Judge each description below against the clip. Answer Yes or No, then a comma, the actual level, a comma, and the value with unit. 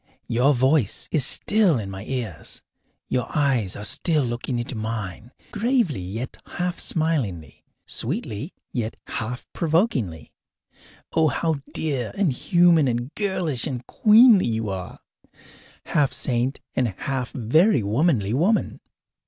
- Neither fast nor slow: No, slow, 125 wpm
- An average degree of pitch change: No, wide, 6.4 semitones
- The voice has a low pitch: Yes, low, 130 Hz